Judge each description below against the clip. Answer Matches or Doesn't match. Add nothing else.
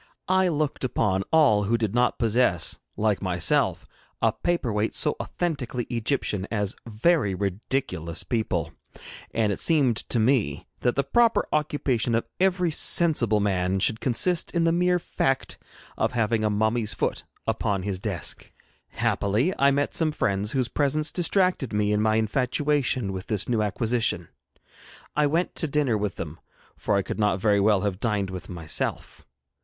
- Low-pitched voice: Matches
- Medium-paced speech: Matches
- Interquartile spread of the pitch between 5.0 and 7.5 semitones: Matches